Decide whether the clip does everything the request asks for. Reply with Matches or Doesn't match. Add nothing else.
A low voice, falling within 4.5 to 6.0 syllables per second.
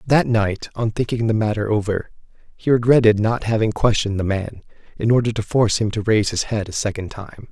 Matches